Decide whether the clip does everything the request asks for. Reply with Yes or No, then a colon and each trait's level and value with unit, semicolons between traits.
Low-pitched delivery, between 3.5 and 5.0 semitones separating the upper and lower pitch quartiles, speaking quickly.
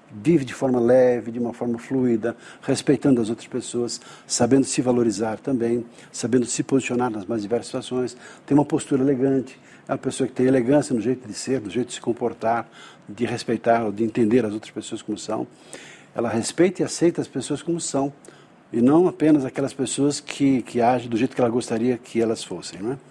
No: low, 125 Hz; average, 2.7 semitones; fast, 200 wpm